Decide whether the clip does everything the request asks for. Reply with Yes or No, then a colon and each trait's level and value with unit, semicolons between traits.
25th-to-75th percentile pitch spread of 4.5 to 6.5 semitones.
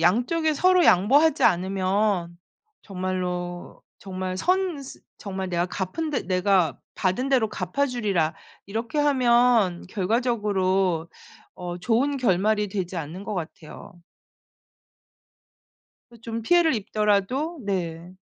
Yes: average, 5.3 semitones